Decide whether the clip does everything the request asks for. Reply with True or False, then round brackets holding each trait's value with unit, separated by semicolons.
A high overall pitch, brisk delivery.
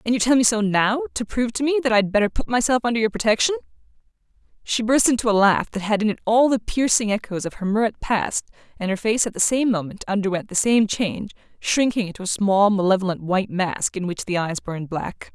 True (215 Hz; 230 wpm)